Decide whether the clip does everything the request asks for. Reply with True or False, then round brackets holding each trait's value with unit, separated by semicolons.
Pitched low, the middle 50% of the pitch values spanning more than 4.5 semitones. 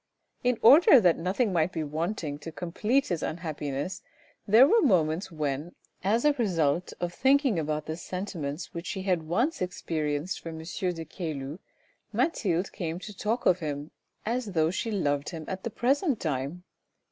False (175 Hz; 5.1 semitones)